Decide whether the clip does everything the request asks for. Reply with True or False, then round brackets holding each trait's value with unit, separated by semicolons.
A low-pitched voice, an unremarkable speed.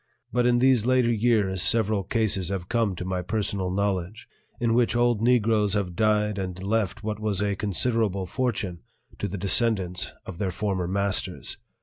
True (105 Hz; 165 wpm)